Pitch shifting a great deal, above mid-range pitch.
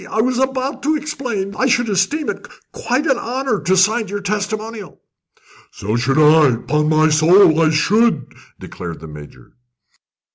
Yes: wide, 7.8 semitones; high, 200 Hz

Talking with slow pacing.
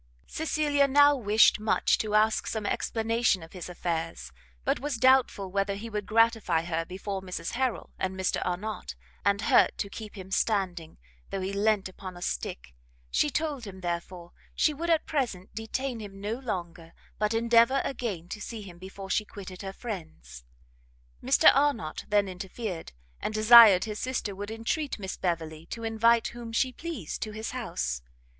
No: average, 170 wpm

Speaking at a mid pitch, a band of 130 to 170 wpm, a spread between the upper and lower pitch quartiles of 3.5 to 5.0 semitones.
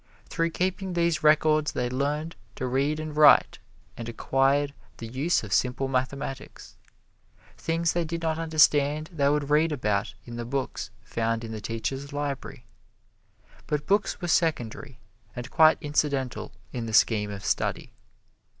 Yes: medium, 145 Hz; average, 150 wpm; average, 4.1 semitones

